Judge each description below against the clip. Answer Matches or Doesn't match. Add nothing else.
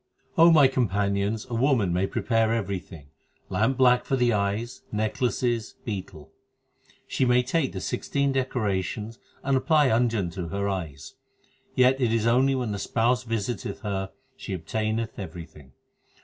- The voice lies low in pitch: Matches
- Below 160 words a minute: Matches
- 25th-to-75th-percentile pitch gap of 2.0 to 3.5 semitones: Doesn't match